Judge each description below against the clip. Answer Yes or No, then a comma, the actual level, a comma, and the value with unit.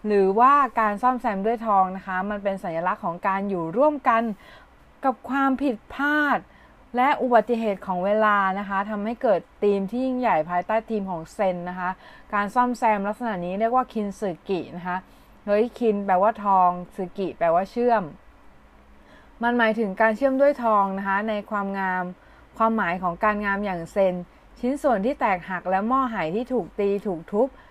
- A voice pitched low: No, high, 205 Hz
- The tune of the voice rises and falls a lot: No, average, 4.0 semitones